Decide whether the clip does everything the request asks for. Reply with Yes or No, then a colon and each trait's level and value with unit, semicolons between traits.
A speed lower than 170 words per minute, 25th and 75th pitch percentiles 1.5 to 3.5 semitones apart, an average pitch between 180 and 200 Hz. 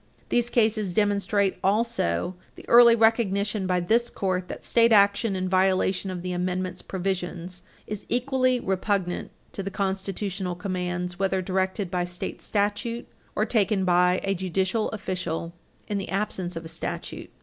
Yes: average, 145 wpm; average, 2.7 semitones; high, 190 Hz